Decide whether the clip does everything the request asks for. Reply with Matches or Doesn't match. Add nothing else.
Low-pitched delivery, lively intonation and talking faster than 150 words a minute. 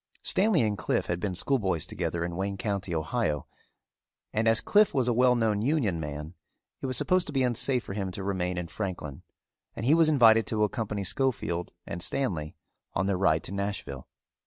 Matches